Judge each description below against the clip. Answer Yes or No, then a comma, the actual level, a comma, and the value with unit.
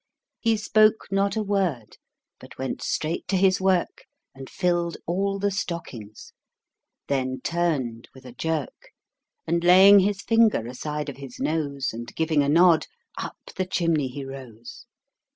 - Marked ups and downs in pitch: Yes, wide, 6.3 semitones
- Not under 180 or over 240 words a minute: No, average, 150 wpm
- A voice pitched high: No, medium, 165 Hz